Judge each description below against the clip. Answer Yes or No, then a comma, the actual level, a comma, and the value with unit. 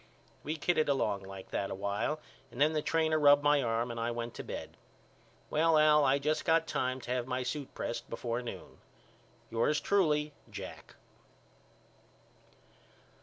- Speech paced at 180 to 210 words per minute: No, average, 160 wpm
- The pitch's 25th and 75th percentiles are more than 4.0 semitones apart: Yes, average, 4.5 semitones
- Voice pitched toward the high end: No, medium, 140 Hz